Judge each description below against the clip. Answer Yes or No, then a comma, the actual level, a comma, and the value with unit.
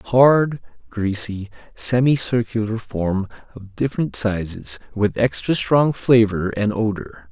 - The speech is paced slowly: Yes, slow, 105 wpm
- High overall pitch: No, low, 110 Hz